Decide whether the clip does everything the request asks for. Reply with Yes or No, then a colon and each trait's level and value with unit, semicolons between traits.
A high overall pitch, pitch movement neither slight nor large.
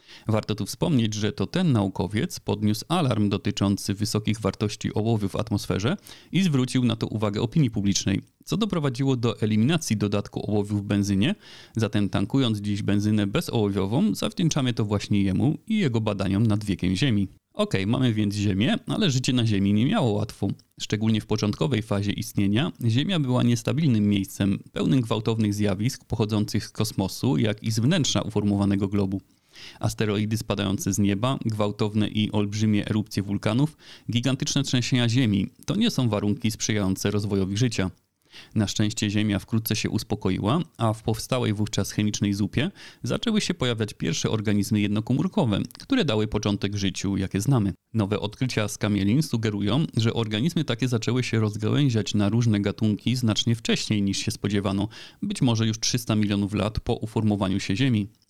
No: low, 110 Hz; average, 3.4 semitones